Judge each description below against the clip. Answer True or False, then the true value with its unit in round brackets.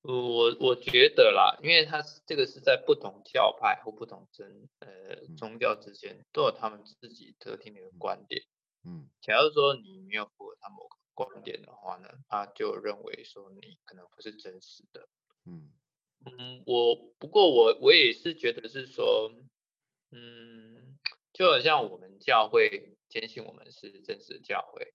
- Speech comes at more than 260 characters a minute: False (240 characters per minute)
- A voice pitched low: False (400 Hz)